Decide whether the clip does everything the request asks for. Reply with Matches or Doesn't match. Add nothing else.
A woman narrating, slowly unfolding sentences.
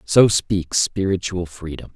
Doesn't match